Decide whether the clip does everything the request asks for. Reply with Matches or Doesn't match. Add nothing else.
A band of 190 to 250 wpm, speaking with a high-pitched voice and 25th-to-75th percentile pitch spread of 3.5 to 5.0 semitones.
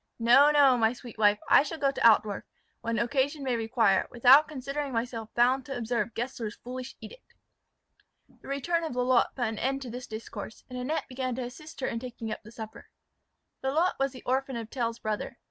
Doesn't match